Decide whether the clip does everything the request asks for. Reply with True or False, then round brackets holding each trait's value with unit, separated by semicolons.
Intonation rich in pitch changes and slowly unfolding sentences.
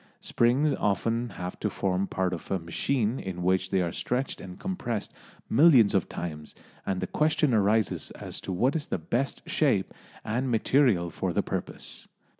False (6.0 semitones; 170 wpm)